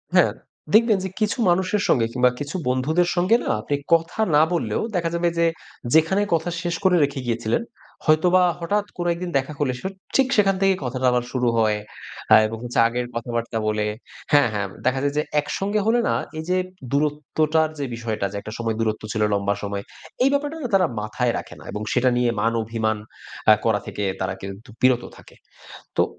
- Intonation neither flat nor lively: No, wide, 7.3 semitones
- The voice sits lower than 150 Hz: Yes, medium, 140 Hz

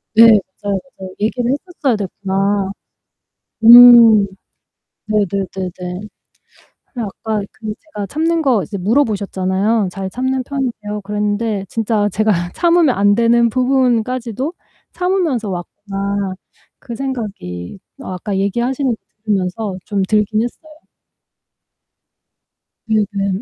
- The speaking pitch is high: Yes, high, 215 Hz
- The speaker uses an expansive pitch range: No, average, 3.6 semitones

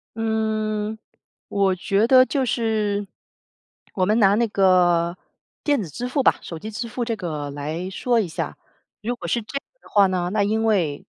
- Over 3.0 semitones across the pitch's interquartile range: Yes, average, 3.6 semitones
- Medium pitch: No, high, 210 Hz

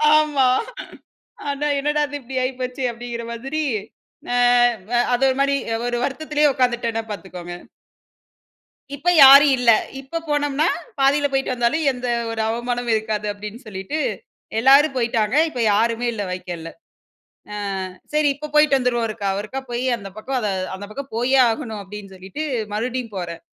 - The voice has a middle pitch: No, high, 245 Hz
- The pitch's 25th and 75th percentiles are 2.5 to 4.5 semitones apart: Yes, average, 4.2 semitones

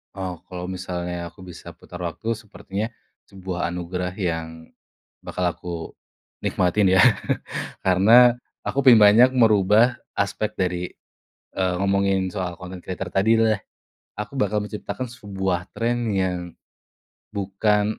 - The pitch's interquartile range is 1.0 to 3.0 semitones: Yes, average, 2.7 semitones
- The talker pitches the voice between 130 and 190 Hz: No, very low, 95 Hz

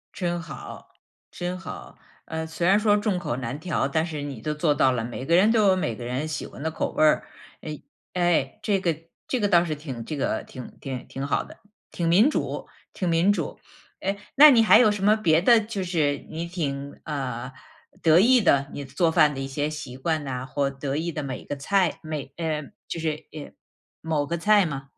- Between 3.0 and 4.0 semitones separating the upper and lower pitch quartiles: No, average, 4.6 semitones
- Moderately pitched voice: Yes, medium, 160 Hz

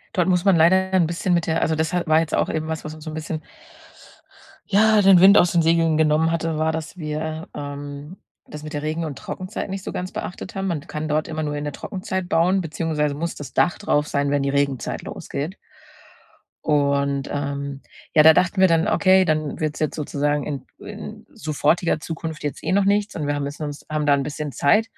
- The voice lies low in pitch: No, medium, 155 Hz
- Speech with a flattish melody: No, average, 3.0 semitones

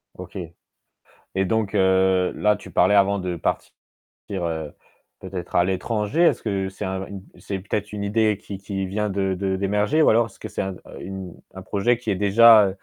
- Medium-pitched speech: No, low, 100 Hz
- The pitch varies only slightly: Yes, narrow, 1.8 semitones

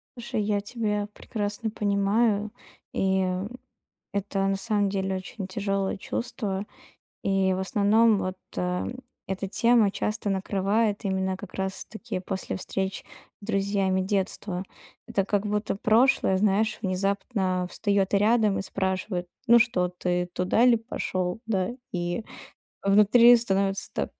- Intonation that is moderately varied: No, narrow, 2.0 semitones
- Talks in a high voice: Yes, high, 200 Hz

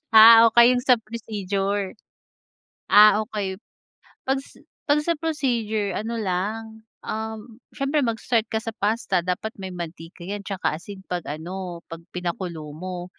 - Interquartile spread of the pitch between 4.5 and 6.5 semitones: No, average, 3.7 semitones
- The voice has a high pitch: Yes, high, 210 Hz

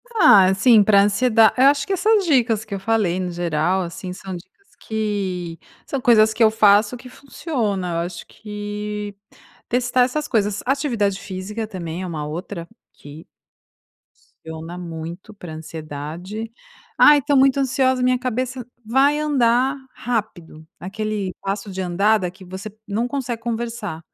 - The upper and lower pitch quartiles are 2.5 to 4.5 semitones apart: No, average, 5.1 semitones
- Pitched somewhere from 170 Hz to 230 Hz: Yes, high, 210 Hz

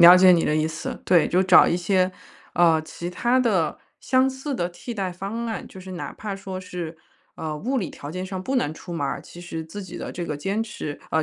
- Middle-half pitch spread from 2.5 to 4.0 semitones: Yes, average, 3.3 semitones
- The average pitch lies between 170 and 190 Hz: Yes, medium, 185 Hz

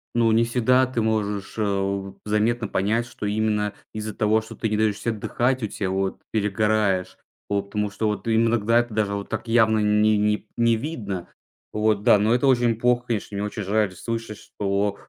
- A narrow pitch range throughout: Yes, narrow, 2.1 semitones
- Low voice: Yes, low, 110 Hz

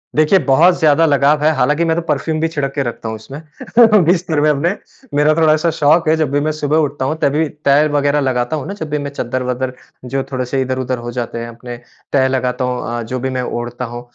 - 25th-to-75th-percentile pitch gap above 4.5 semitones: No, average, 3.6 semitones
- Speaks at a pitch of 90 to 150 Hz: Yes, medium, 140 Hz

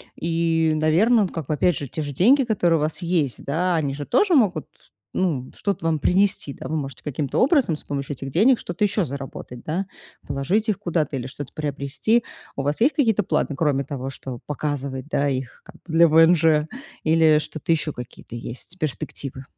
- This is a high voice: No, medium, 155 Hz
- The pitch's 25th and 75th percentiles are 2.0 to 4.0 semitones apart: No, average, 4.4 semitones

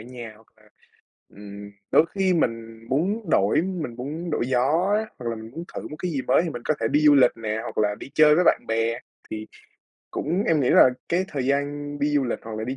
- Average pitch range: No, wide, 5.7 semitones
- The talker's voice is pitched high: No, low, 135 Hz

